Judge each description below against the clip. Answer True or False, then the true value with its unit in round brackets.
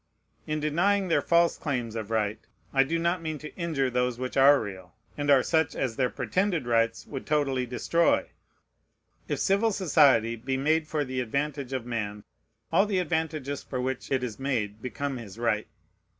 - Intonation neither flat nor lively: True (5.0 semitones)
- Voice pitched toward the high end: False (135 Hz)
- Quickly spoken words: False (180 wpm)